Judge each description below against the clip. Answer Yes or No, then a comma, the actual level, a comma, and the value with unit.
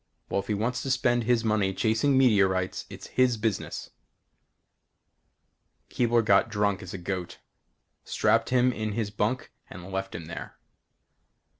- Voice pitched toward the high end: No, low, 110 Hz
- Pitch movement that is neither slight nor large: Yes, average, 3.7 semitones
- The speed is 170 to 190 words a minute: No, average, 145 wpm